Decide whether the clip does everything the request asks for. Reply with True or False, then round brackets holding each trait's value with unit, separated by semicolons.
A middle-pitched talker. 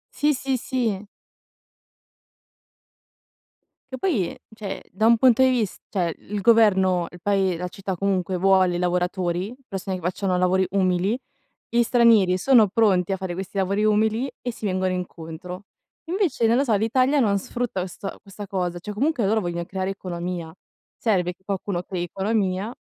False (195 Hz)